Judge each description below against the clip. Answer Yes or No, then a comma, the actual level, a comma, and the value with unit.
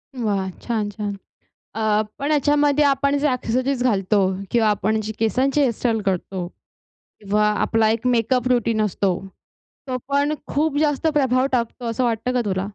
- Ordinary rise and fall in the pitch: Yes, average, 4.3 semitones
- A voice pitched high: Yes, high, 235 Hz